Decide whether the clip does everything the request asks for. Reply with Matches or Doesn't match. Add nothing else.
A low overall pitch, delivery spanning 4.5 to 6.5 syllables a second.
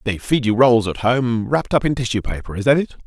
Matches